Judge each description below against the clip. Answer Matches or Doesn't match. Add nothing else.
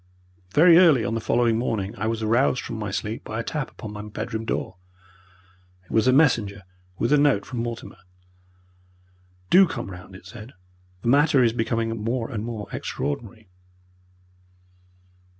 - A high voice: Doesn't match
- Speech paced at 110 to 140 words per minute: Doesn't match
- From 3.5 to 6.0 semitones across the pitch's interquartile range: Doesn't match